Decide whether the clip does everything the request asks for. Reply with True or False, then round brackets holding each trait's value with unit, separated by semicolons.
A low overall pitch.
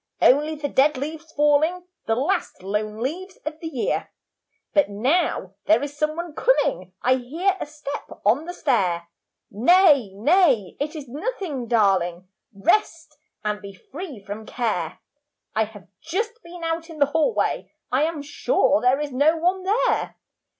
False (290 Hz)